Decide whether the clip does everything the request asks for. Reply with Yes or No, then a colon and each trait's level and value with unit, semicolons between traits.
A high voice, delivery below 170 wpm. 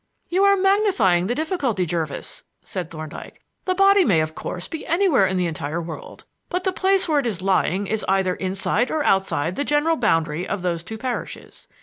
No: high, 200 Hz; average, 195 wpm